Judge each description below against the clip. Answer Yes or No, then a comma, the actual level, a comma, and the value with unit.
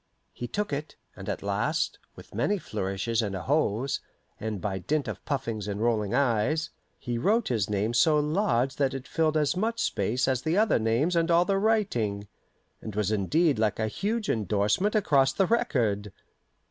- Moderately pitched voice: No, low, 130 Hz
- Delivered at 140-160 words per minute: No, average, 175 wpm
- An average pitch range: No, wide, 7.4 semitones